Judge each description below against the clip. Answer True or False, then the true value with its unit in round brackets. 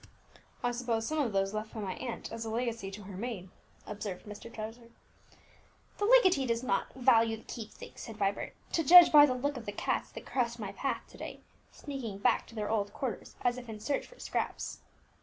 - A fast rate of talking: True (210 wpm)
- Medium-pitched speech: False (230 Hz)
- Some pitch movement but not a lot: True (3.3 semitones)